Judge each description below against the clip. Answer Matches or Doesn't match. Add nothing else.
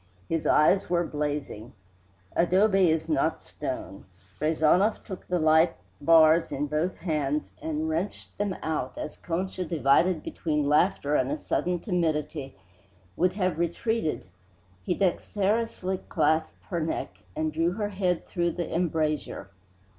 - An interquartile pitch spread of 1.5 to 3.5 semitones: Matches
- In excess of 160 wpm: Doesn't match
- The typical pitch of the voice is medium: Matches